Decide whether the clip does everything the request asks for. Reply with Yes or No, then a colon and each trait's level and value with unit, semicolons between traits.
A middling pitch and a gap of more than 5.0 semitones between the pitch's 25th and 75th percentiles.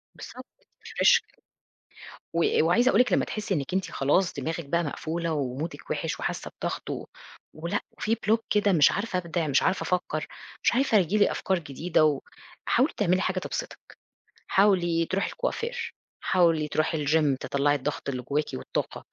No: medium, 170 Hz; average, 4.6 semitones